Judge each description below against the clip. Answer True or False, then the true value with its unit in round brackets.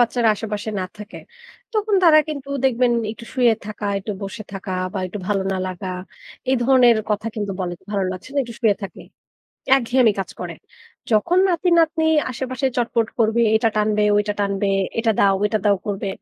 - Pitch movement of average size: True (3.7 semitones)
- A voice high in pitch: True (220 Hz)